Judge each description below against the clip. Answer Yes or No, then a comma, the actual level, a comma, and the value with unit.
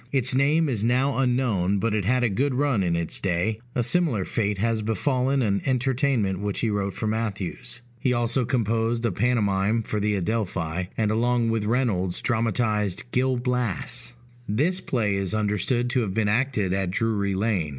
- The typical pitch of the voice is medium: No, low, 115 Hz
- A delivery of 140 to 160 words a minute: No, average, 175 wpm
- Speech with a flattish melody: No, average, 3.8 semitones